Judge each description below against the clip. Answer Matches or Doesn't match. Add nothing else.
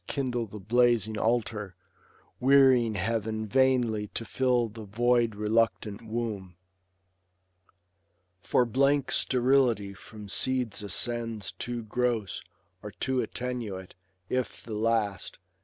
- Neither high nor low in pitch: Doesn't match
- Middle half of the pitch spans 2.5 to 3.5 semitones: Matches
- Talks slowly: Matches